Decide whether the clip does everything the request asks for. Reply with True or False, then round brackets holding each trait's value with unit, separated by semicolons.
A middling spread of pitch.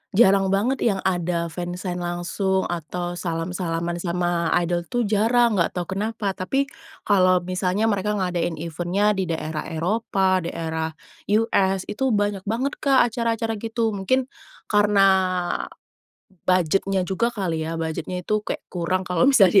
True (3.2 semitones)